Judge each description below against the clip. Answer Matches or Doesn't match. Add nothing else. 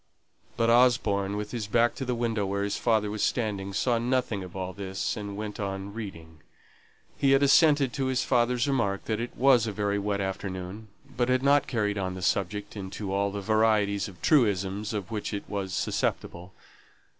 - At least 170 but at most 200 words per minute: Matches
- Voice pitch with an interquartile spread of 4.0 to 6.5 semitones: Doesn't match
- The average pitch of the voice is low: Matches